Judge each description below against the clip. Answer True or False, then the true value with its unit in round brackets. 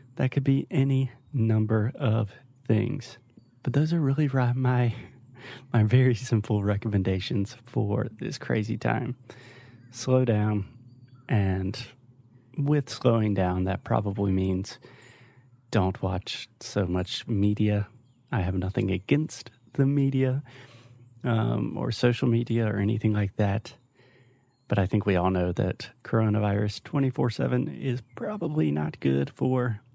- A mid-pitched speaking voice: False (120 Hz)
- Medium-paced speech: True (130 wpm)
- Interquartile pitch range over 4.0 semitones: False (3.4 semitones)